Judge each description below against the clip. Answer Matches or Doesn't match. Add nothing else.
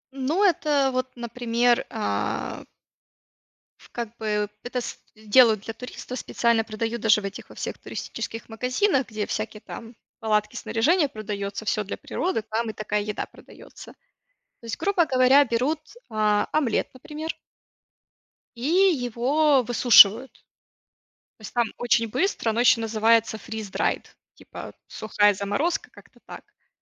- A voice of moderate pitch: Doesn't match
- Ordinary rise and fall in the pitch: Matches